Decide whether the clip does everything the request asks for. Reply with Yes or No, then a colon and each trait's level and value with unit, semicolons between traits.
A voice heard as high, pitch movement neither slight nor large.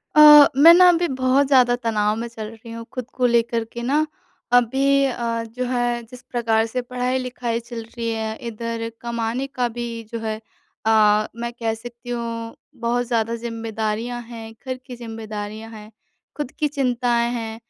No: high, 235 Hz; narrow, 1.7 semitones